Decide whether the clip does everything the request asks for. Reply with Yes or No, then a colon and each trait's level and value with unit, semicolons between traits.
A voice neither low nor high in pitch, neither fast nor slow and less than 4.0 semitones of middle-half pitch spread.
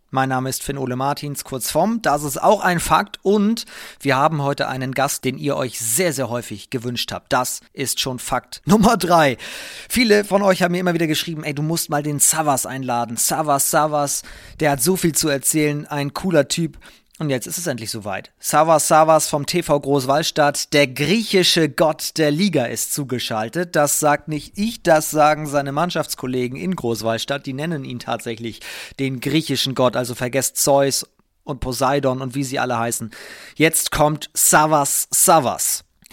Yes: medium, 145 Hz; average, 180 wpm; average, 3.5 semitones